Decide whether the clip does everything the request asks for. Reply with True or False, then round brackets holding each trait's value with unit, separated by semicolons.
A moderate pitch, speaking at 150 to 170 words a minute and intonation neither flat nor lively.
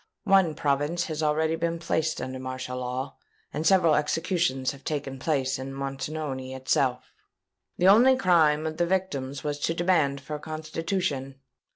True (150 Hz; 155 wpm; 3.6 semitones)